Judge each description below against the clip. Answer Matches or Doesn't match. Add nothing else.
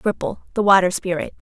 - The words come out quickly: Doesn't match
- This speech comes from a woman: Matches